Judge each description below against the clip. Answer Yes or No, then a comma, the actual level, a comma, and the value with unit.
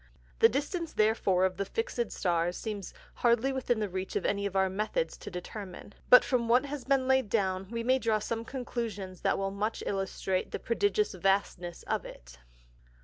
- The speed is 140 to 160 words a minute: No, average, 185 wpm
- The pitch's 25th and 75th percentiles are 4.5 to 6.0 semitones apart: Yes, average, 4.8 semitones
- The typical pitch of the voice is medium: No, high, 215 Hz